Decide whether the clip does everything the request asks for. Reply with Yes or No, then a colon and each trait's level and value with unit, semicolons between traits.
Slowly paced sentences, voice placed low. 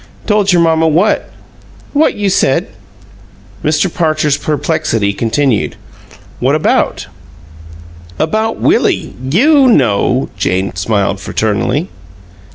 No: slow, 95 wpm; medium, 155 Hz